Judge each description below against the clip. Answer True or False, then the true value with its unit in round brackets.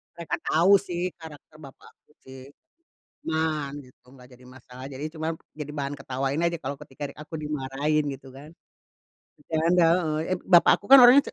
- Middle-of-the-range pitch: True (150 Hz)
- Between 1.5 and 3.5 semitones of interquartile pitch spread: True (3.2 semitones)